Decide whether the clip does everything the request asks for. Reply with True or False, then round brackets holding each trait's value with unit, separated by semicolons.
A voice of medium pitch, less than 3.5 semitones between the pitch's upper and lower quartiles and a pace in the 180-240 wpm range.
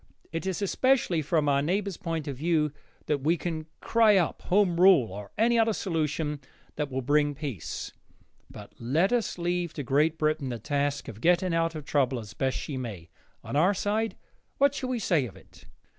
False (155 Hz; 4.8 semitones; 190 wpm)